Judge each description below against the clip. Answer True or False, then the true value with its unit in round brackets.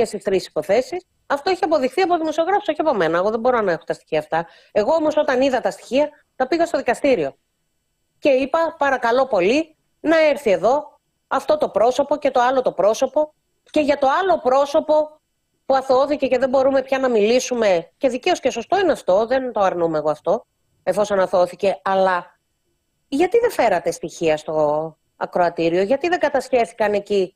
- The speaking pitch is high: True (265 Hz)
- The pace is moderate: False (180 wpm)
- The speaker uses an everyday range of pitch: False (7.7 semitones)